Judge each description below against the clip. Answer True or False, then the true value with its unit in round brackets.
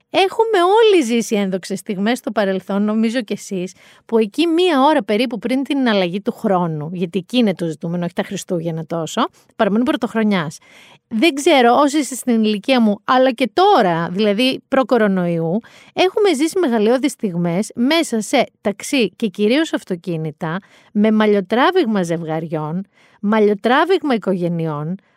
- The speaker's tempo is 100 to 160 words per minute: True (140 wpm)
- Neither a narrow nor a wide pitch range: False (5.7 semitones)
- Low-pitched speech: False (220 Hz)